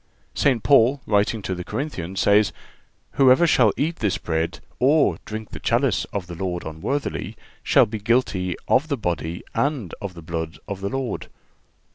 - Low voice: Yes, low, 105 Hz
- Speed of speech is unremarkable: Yes, average, 165 wpm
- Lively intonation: Yes, wide, 6.8 semitones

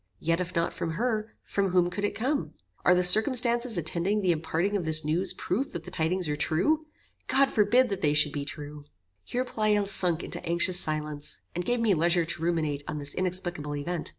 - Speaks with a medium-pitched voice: Yes, medium, 175 Hz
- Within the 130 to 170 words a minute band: No, fast, 205 wpm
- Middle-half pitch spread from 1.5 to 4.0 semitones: No, average, 4.6 semitones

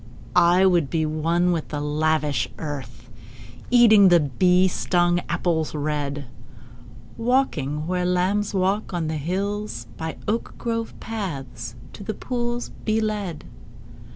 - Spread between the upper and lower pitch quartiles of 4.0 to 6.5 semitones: Yes, average, 5.2 semitones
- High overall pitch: No, medium, 175 Hz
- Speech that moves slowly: Yes, slow, 125 wpm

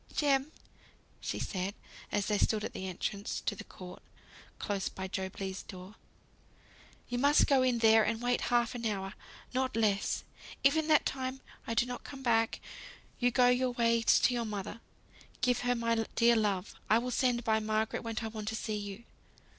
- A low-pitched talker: No, high, 230 Hz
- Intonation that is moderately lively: Yes, average, 3.1 semitones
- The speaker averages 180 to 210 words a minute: Yes, average, 185 wpm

